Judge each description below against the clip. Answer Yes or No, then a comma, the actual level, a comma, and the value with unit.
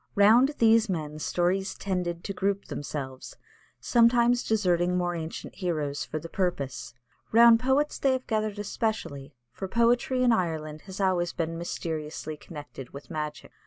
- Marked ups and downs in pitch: Yes, wide, 6.2 semitones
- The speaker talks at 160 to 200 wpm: No, average, 145 wpm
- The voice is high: No, medium, 180 Hz